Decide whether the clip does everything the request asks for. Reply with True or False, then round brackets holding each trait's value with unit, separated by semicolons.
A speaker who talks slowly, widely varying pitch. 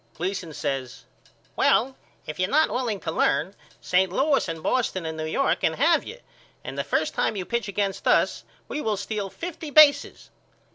False (180 wpm; 6.8 semitones)